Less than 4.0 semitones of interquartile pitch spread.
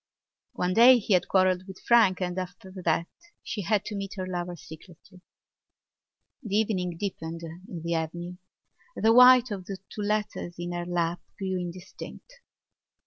Yes: average, 2.9 semitones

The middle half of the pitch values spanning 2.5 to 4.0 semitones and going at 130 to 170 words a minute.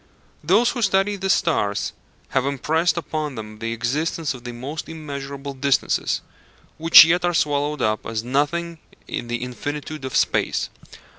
No: average, 4.5 semitones; average, 150 wpm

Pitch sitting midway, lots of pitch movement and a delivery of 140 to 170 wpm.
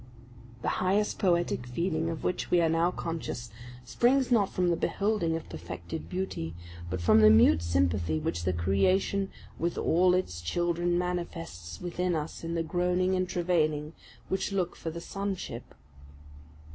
Yes: medium, 170 Hz; wide, 7.7 semitones; average, 155 wpm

